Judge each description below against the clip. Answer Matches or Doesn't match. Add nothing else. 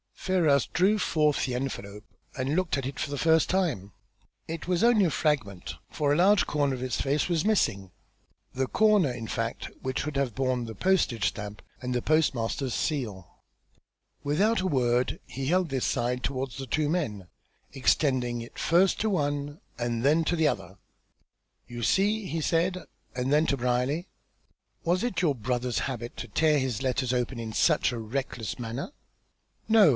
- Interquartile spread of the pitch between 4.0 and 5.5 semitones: Matches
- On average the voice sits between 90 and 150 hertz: Matches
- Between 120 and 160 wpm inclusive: Doesn't match